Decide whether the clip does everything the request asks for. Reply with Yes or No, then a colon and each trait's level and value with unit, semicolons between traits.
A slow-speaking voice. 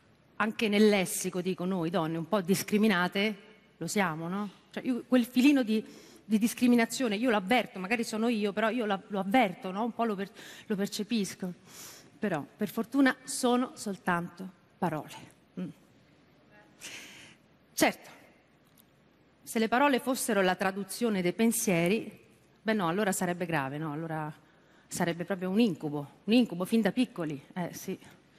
No: average, 150 wpm